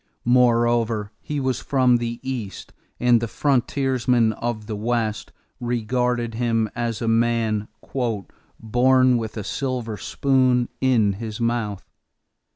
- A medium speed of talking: No, slow, 120 wpm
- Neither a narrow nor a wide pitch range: No, narrow, 2.0 semitones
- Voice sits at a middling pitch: No, low, 120 Hz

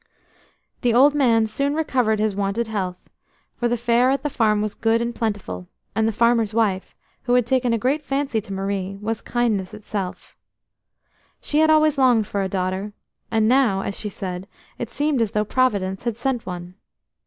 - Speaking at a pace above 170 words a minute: Yes, average, 185 wpm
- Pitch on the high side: Yes, high, 225 Hz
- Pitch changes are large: No, average, 3.7 semitones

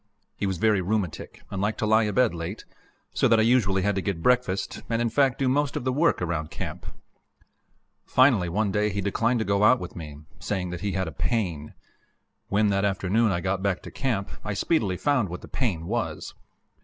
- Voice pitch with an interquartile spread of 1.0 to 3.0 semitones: No, average, 3.8 semitones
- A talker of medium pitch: No, low, 100 Hz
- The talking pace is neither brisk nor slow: No, fast, 210 wpm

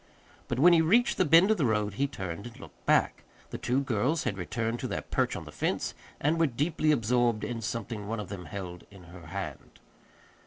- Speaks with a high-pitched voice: No, low, 120 Hz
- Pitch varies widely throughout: Yes, wide, 6.5 semitones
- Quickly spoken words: Yes, fast, 220 wpm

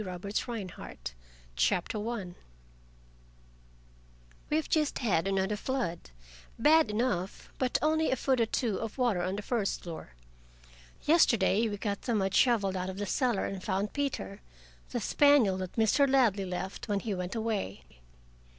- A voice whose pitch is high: Yes, high, 210 Hz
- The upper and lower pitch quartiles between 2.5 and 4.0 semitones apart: No, average, 4.6 semitones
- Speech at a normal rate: Yes, average, 155 wpm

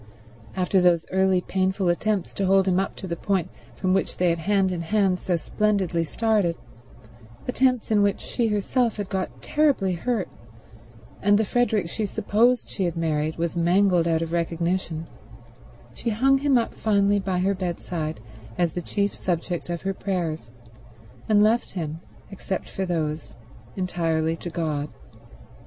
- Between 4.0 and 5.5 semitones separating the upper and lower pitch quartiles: No, average, 3.2 semitones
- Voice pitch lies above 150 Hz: Yes, medium, 185 Hz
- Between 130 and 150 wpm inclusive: No, average, 160 wpm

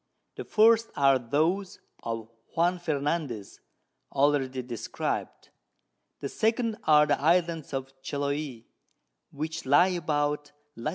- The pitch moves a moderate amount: Yes, average, 4.1 semitones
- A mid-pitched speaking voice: Yes, medium, 145 Hz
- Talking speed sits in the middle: No, slow, 110 wpm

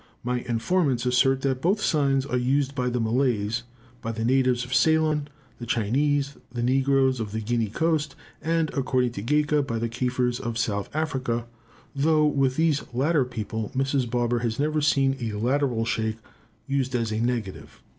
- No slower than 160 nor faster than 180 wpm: Yes, average, 170 wpm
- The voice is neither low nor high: No, low, 130 Hz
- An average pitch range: Yes, average, 3.2 semitones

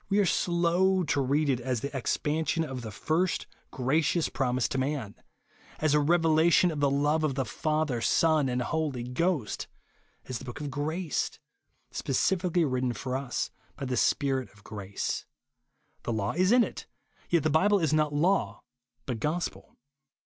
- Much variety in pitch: No, average, 4.3 semitones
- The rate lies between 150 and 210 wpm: Yes, average, 170 wpm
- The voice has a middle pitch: Yes, medium, 145 Hz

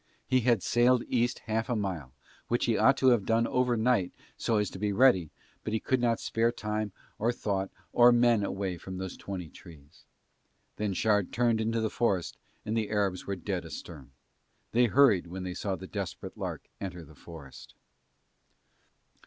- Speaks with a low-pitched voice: Yes, low, 105 Hz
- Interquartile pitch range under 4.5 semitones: Yes, average, 4.1 semitones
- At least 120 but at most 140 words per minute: No, average, 180 wpm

